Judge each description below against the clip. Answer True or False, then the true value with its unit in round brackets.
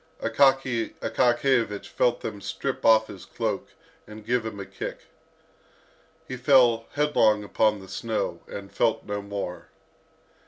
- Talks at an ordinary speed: False (130 wpm)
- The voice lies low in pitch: True (115 Hz)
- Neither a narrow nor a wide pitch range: True (3.1 semitones)